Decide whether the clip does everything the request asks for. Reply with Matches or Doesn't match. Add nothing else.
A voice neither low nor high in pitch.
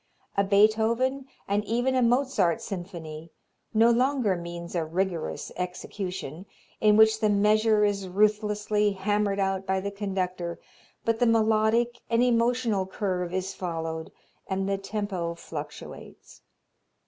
Doesn't match